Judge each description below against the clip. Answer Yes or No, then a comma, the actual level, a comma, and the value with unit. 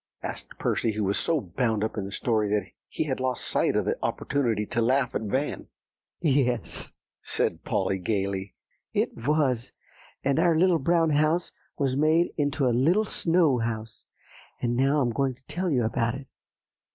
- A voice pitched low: Yes, low, 130 Hz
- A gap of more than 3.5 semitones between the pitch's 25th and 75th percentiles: Yes, average, 5.3 semitones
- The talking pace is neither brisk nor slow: Yes, average, 170 wpm